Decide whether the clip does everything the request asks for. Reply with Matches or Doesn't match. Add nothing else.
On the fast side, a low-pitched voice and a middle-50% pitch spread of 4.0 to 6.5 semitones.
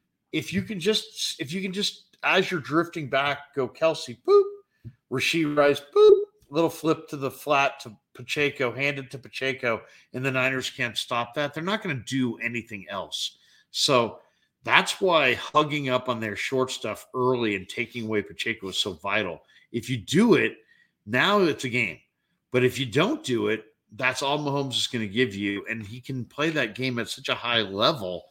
Doesn't match